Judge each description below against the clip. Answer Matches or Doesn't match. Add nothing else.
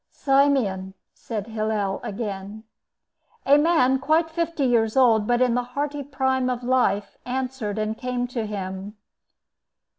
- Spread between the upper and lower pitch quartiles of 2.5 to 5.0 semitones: Matches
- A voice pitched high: Matches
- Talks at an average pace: Doesn't match